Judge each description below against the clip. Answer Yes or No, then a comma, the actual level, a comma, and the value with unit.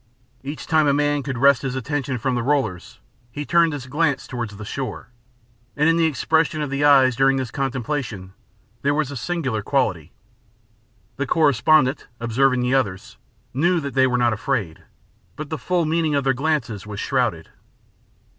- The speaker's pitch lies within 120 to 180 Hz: Yes, low, 135 Hz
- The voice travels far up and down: No, average, 3.3 semitones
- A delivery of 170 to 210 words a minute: Yes, average, 175 wpm